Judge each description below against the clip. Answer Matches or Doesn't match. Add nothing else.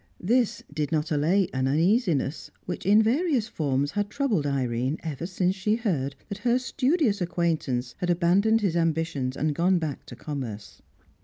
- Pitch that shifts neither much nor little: Doesn't match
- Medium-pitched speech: Matches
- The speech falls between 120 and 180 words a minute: Matches